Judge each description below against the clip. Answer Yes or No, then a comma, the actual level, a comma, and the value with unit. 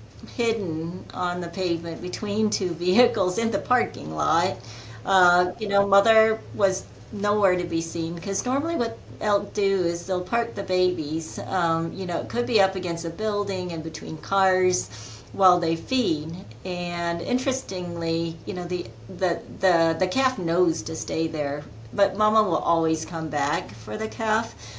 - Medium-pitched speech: Yes, medium, 180 Hz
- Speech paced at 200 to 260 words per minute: No, average, 165 wpm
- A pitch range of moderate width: Yes, average, 3.4 semitones